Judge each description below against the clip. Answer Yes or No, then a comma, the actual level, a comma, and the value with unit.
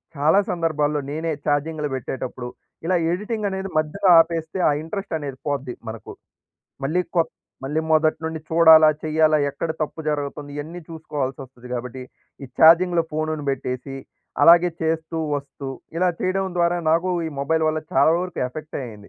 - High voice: No, medium, 155 Hz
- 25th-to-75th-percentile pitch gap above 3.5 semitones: No, average, 2.7 semitones